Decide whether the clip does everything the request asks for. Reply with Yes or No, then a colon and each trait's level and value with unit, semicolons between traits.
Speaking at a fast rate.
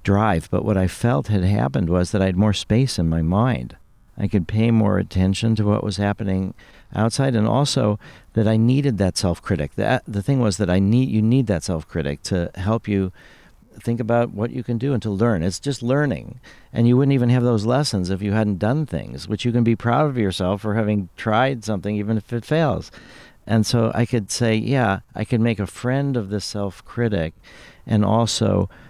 Yes: fast, 210 wpm